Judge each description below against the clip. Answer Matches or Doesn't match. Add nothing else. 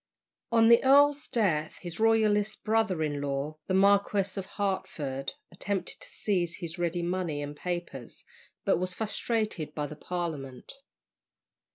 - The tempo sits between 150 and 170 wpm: Doesn't match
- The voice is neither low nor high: Matches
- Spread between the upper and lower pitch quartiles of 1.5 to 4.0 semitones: Doesn't match